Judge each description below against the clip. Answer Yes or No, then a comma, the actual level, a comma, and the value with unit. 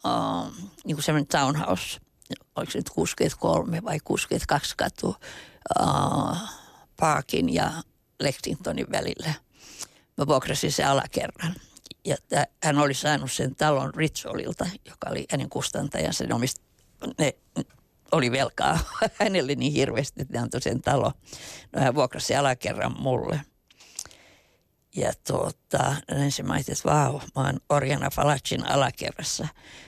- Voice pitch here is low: No, medium, 145 Hz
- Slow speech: No, average, 125 wpm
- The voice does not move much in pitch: Yes, narrow, 1.7 semitones